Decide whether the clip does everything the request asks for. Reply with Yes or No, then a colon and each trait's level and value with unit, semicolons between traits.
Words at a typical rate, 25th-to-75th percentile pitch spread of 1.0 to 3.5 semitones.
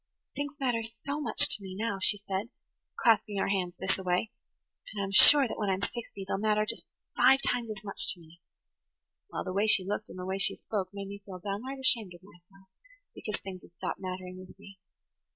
No: fast, 215 wpm; average, 2.9 semitones